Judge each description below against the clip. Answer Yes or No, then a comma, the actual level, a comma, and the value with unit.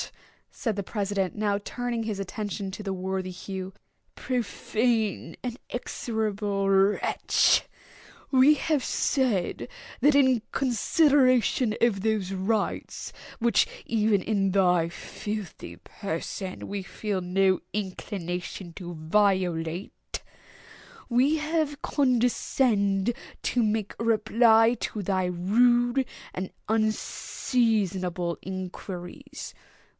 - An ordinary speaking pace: No, slow, 95 wpm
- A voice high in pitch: Yes, high, 210 Hz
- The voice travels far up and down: No, average, 4.0 semitones